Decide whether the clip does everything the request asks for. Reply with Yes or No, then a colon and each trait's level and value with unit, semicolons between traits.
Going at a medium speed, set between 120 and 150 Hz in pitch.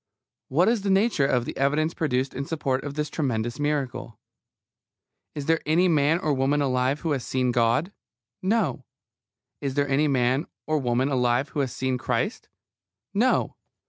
Yes: average, 165 wpm; medium, 140 Hz